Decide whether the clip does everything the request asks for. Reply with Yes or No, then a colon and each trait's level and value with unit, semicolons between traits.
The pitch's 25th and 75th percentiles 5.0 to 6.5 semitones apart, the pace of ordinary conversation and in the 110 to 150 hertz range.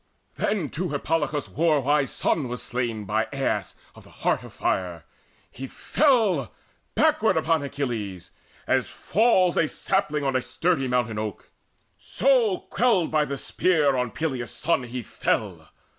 Yes: average, 5.3 semitones; average, 150 wpm; medium, 140 Hz